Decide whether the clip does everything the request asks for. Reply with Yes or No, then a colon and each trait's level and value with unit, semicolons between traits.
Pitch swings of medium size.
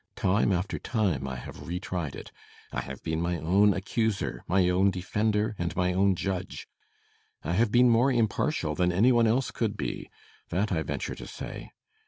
Yes: average, 3.8 semitones